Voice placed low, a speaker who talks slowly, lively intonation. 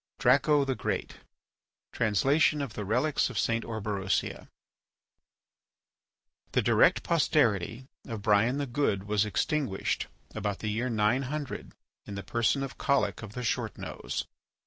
No: low, 115 Hz; slow, 130 wpm; average, 4.6 semitones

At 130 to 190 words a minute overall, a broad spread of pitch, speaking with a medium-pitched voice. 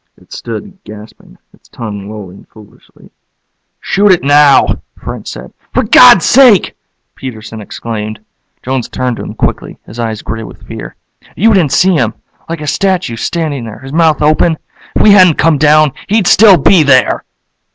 Yes: average, 160 wpm; wide, 7.8 semitones; medium, 145 Hz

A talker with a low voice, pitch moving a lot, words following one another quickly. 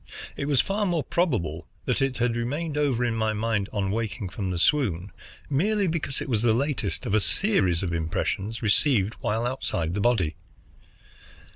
No: low, 115 Hz; wide, 6.3 semitones; average, 175 wpm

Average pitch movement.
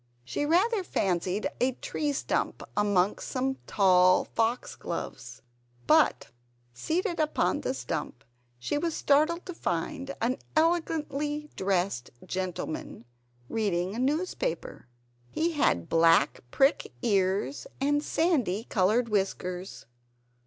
No: wide, 8.5 semitones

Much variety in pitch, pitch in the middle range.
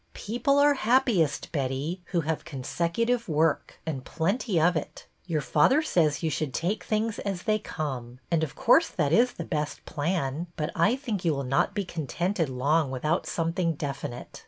Yes: wide, 5.8 semitones; medium, 165 Hz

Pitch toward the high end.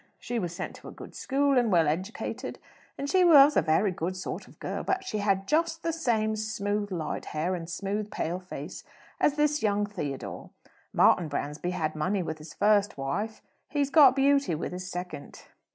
Yes: high, 205 Hz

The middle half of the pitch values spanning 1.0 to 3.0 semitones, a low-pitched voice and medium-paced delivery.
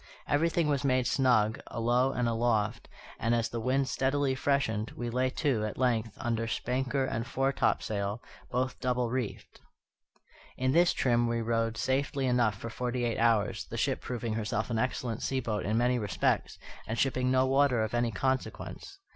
Yes: narrow, 2.5 semitones; low, 120 Hz; average, 170 wpm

